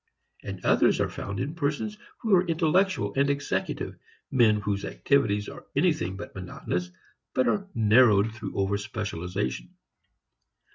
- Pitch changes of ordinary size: No, wide, 6.2 semitones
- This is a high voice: No, low, 110 Hz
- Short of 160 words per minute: Yes, slow, 135 wpm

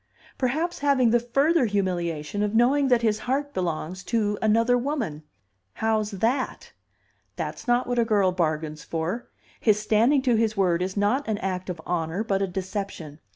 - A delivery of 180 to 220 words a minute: No, average, 165 wpm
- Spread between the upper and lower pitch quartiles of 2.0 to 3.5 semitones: No, average, 5.0 semitones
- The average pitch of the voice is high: Yes, high, 215 Hz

